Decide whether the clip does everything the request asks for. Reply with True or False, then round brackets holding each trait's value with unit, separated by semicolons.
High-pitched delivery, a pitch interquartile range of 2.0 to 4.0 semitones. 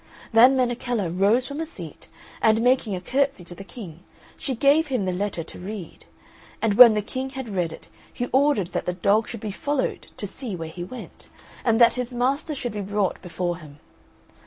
False (220 Hz; 5.6 semitones)